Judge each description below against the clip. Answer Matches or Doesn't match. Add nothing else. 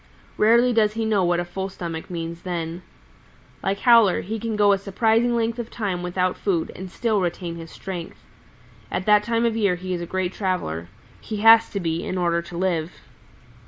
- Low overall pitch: Doesn't match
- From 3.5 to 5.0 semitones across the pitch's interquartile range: Matches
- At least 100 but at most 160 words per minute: Doesn't match